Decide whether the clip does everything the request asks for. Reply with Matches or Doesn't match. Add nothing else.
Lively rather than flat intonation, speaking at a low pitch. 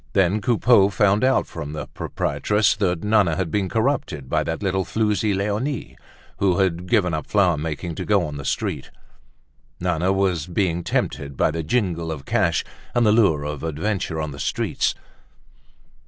Doesn't match